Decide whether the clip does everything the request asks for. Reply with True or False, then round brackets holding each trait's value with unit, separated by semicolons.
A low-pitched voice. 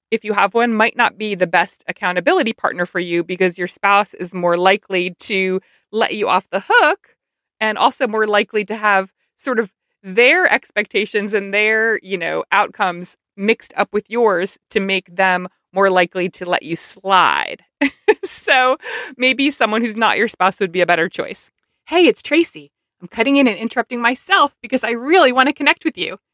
False (210 Hz)